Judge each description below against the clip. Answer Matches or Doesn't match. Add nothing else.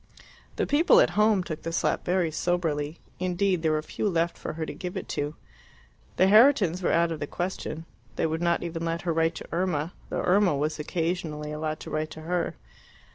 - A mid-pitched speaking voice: Matches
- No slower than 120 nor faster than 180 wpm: Doesn't match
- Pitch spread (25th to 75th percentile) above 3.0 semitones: Doesn't match